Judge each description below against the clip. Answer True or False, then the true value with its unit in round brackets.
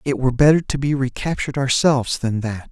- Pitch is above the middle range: False (135 Hz)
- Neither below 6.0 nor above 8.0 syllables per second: True (6.1 syllables/s)